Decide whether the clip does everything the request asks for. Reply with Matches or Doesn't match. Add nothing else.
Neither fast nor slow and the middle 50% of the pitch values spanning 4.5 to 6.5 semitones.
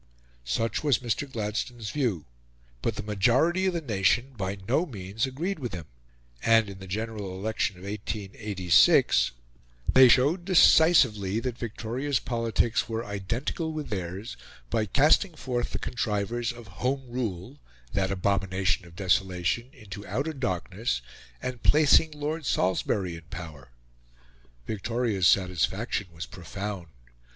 Doesn't match